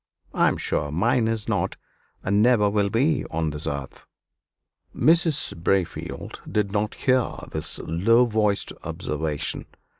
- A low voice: Yes, low, 105 Hz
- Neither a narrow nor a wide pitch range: No, wide, 6.4 semitones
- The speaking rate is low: Yes, slow, 130 wpm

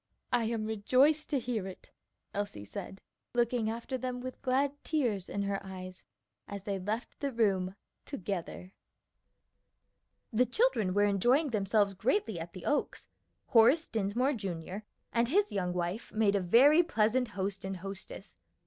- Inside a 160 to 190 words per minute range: No, average, 150 wpm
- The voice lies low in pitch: No, high, 215 Hz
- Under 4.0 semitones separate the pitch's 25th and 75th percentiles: No, average, 4.6 semitones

